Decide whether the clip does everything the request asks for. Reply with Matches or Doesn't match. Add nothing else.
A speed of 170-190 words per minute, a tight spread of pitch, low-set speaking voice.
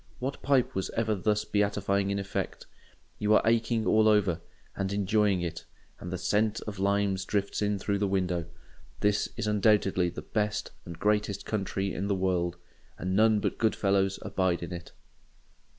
Matches